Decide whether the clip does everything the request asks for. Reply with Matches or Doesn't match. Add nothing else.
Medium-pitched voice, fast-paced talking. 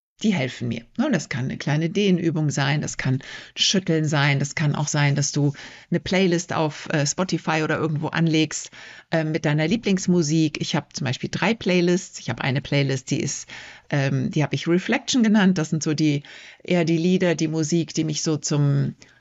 Matches